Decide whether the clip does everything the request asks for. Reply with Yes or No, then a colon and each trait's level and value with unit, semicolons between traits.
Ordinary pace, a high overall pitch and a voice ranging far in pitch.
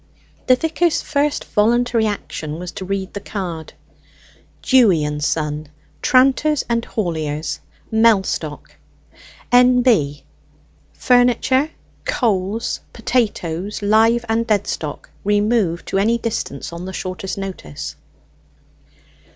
No: slow, 100 wpm; high, 210 Hz; wide, 5.8 semitones